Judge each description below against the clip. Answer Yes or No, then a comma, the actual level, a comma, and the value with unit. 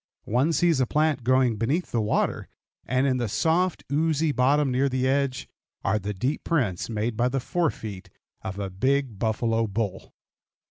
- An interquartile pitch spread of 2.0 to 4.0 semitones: No, average, 4.5 semitones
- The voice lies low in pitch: Yes, low, 130 Hz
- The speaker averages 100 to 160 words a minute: No, average, 175 wpm